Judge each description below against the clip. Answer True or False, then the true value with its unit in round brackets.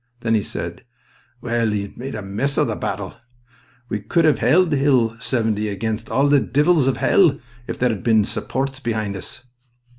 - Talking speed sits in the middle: True (175 wpm)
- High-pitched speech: False (120 Hz)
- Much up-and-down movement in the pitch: False (4.2 semitones)